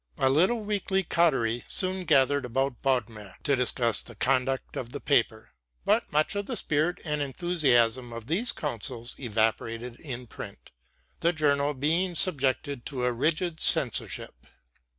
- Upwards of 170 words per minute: No, average, 145 wpm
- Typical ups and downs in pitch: Yes, average, 5.0 semitones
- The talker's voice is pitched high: No, low, 135 Hz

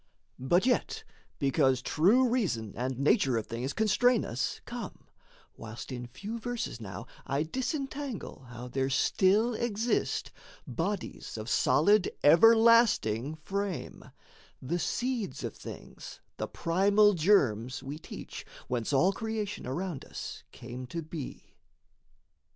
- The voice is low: No, medium, 165 Hz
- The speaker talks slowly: Yes, slow, 120 wpm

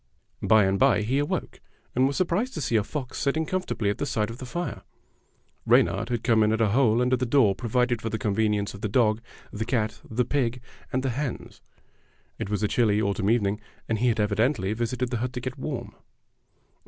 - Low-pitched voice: Yes, low, 115 Hz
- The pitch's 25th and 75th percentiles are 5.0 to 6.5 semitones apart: No, average, 3.2 semitones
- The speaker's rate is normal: No, fast, 215 wpm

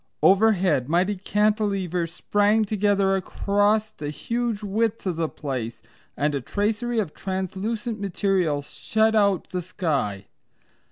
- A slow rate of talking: Yes, slow, 120 wpm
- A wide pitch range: No, average, 3.8 semitones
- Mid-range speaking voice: No, high, 195 Hz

